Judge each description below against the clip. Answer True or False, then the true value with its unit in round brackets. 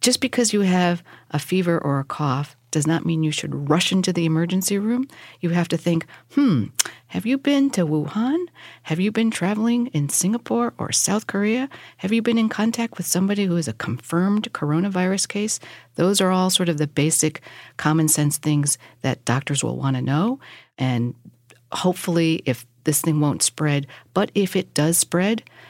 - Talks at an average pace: True (185 wpm)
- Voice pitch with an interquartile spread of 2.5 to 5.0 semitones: False (5.4 semitones)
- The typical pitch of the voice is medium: True (170 Hz)